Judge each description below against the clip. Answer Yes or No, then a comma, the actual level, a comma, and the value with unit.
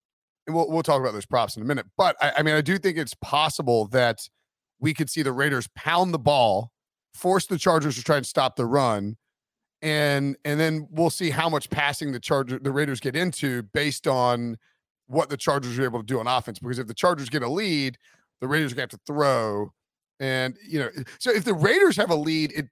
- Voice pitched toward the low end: No, medium, 145 Hz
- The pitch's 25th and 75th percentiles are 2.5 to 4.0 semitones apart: Yes, average, 3.6 semitones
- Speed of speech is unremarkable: No, fast, 225 wpm